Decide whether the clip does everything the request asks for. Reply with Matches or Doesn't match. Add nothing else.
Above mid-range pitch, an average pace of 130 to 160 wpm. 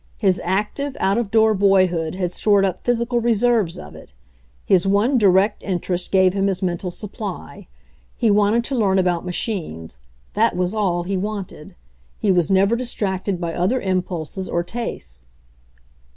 Matches